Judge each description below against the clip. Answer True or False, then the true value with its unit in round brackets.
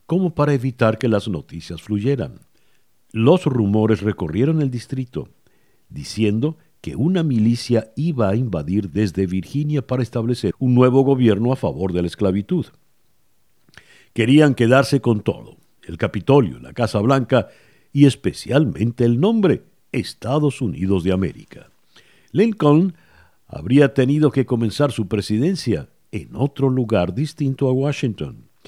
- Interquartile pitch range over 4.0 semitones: True (4.8 semitones)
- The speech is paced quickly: False (130 wpm)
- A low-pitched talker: True (125 Hz)